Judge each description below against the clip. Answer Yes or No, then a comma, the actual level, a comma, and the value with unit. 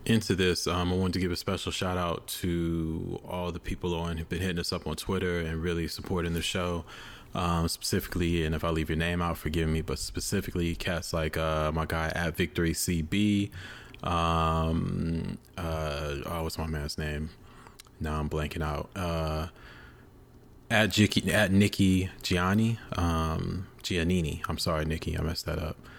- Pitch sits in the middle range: No, very low, 85 Hz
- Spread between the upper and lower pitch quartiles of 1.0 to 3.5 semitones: Yes, narrow, 2.5 semitones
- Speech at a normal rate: Yes, average, 175 wpm